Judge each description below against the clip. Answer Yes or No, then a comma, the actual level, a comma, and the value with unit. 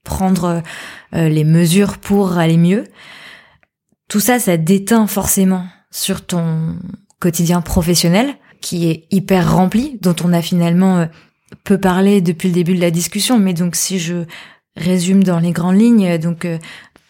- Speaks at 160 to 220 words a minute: No, slow, 145 wpm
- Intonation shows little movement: Yes, narrow, 2.2 semitones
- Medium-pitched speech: Yes, medium, 180 Hz